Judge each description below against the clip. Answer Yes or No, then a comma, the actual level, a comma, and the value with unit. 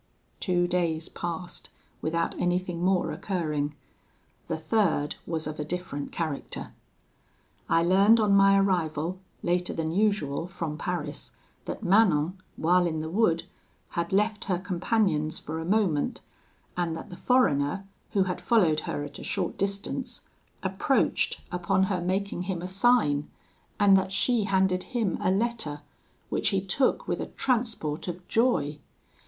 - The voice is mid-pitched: Yes, medium, 180 Hz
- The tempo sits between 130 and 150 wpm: Yes, average, 145 wpm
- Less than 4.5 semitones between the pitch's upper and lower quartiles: Yes, average, 3.6 semitones